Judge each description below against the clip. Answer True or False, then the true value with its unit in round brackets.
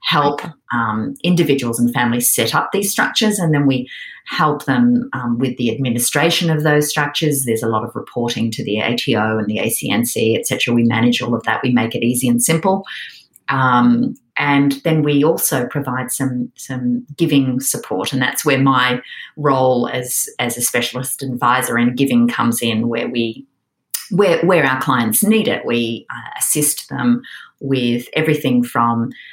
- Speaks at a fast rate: False (170 wpm)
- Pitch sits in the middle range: False (130 Hz)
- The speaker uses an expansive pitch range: False (3.7 semitones)